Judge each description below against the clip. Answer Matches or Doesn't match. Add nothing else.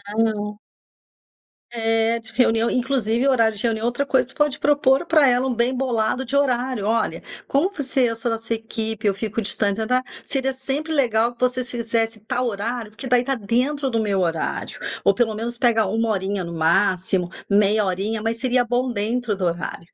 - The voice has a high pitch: Matches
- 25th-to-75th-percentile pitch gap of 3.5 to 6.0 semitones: Doesn't match